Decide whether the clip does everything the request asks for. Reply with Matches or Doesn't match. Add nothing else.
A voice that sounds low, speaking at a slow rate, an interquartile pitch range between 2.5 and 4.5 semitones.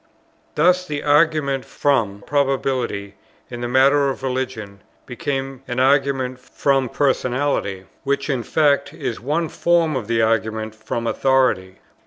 Matches